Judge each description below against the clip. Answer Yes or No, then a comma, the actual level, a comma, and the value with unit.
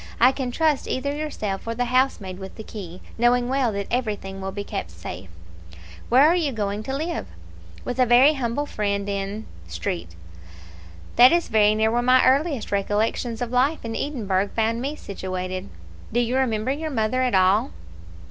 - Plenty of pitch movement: No, average, 4.5 semitones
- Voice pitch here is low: No, high, 230 Hz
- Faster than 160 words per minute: Yes, average, 175 wpm